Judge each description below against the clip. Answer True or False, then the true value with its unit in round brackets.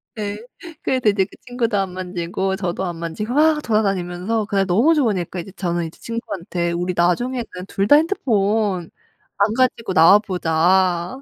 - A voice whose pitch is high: True (195 Hz)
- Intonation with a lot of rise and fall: False (4.2 semitones)